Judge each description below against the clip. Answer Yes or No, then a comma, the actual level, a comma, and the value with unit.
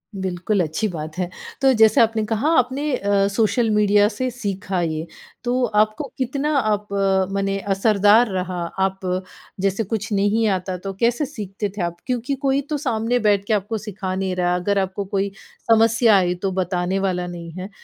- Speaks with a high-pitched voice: Yes, high, 205 Hz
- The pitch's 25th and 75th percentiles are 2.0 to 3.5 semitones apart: Yes, average, 3.2 semitones